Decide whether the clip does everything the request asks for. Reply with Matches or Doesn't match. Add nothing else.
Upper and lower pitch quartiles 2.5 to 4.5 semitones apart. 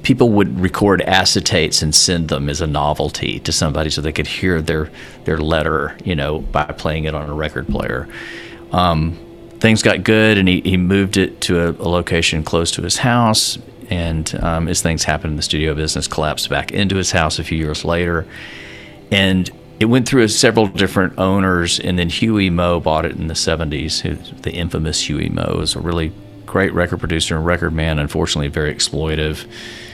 Matches